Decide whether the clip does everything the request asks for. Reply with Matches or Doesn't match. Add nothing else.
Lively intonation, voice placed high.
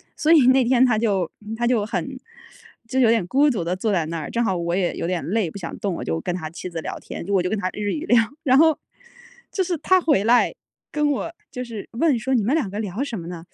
Matches